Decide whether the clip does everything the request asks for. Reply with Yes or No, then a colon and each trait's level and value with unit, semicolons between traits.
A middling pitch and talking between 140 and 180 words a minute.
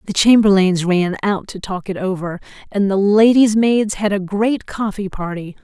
No: high, 200 Hz; average, 170 wpm